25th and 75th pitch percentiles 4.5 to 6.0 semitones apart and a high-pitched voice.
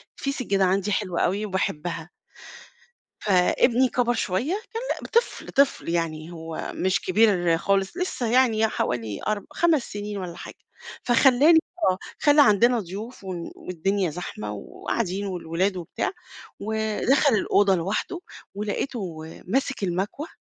Yes: average, 5.2 semitones; high, 200 Hz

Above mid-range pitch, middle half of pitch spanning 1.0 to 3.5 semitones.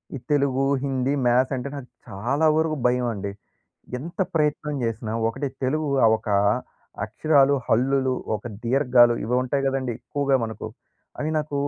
No: low, 130 Hz; average, 2.9 semitones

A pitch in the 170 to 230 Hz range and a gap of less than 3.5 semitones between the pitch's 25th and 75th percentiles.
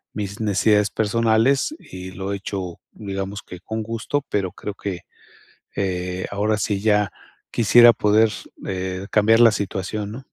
No: low, 105 Hz; narrow, 2.5 semitones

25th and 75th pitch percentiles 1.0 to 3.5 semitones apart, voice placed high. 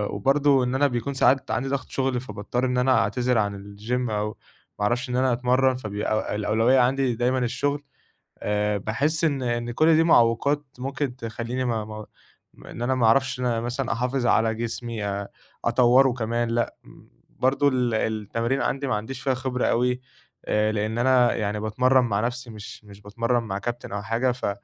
No: average, 3.0 semitones; low, 120 Hz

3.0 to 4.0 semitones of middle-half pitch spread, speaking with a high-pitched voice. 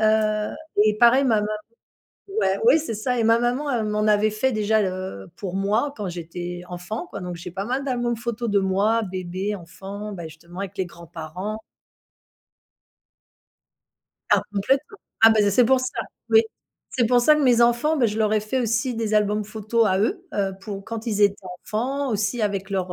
Yes: average, 3.4 semitones; high, 215 Hz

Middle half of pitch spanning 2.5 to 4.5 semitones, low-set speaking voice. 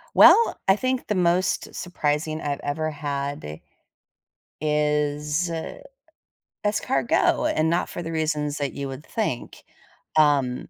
No: average, 2.8 semitones; medium, 150 Hz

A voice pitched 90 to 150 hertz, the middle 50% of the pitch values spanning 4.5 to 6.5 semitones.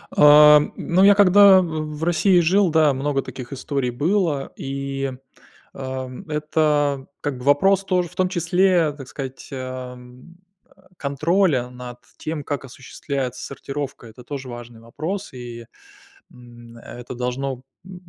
Yes: medium, 140 Hz; average, 4.9 semitones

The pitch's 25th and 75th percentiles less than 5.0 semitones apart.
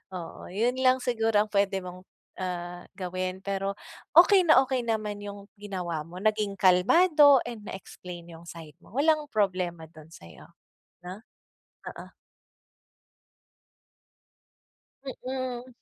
No: wide, 5.5 semitones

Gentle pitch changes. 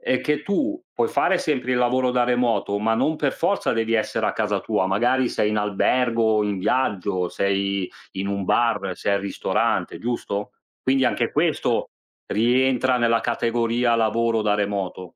No: average, 3.7 semitones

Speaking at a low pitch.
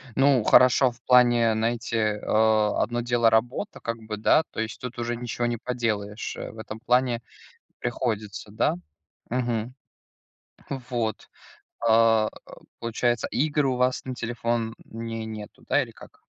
Yes: low, 115 Hz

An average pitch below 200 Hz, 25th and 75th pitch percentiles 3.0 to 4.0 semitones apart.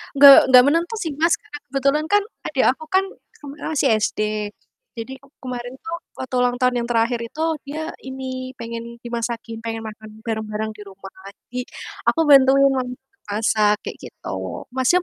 No: very high, 250 Hz; average, 3.5 semitones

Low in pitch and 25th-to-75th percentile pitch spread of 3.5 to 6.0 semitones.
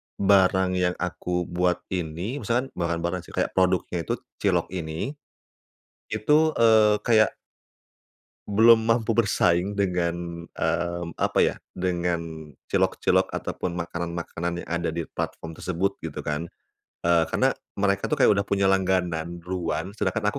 No: very low, 90 Hz; average, 2.9 semitones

